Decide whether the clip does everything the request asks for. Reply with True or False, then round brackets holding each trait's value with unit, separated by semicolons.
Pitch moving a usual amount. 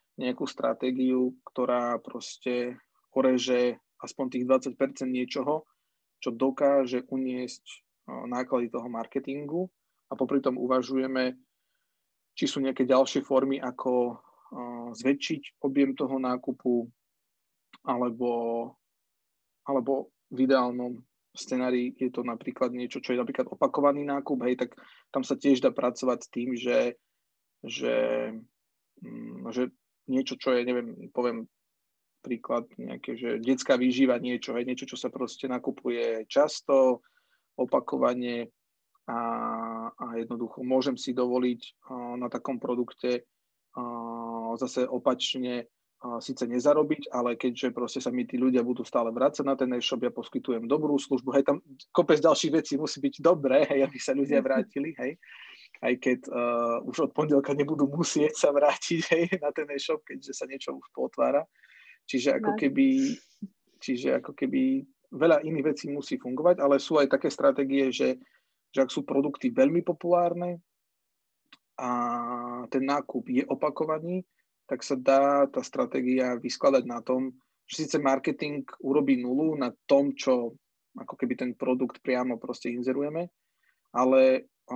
False (2.2 semitones)